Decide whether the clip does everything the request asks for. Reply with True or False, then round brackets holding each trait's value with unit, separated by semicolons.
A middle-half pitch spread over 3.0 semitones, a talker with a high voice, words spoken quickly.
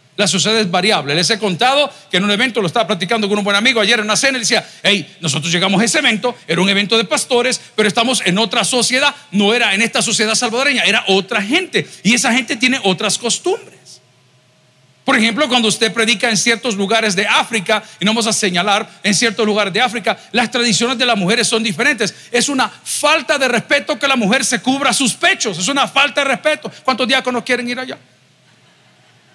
True (3.6 semitones; 230 Hz; 215 wpm)